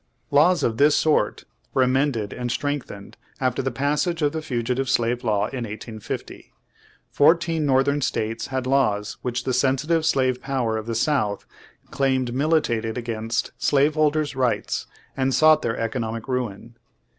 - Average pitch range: Yes, average, 3.8 semitones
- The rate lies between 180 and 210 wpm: No, average, 145 wpm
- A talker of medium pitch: No, low, 130 Hz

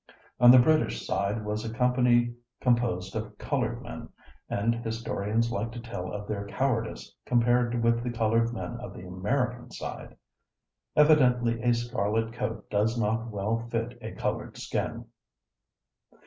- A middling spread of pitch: No, narrow, 2.1 semitones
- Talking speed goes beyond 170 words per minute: No, average, 145 wpm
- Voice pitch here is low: Yes, low, 115 Hz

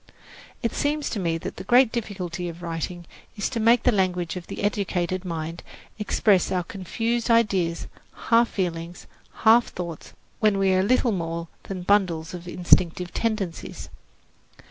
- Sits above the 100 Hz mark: Yes, medium, 185 Hz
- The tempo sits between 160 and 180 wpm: No, average, 150 wpm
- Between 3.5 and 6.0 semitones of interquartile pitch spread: Yes, average, 4.1 semitones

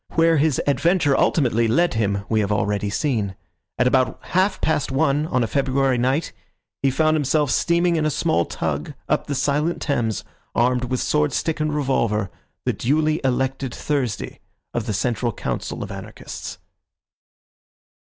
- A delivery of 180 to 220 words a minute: No, average, 150 wpm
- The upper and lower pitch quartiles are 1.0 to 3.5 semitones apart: No, average, 4.7 semitones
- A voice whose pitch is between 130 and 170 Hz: Yes, low, 135 Hz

